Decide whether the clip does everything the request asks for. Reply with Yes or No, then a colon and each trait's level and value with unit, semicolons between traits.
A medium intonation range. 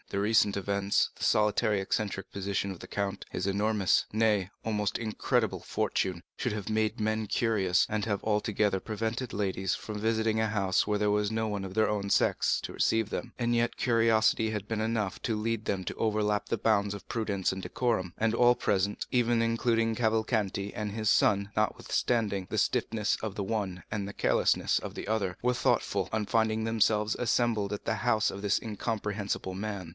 No: narrow, 1.9 semitones